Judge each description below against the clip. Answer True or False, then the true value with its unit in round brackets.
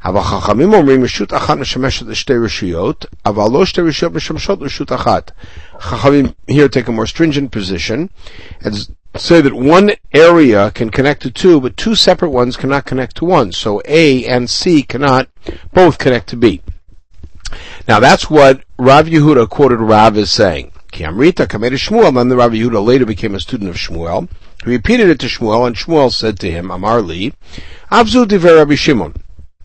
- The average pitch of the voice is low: True (125 Hz)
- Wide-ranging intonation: True (6.8 semitones)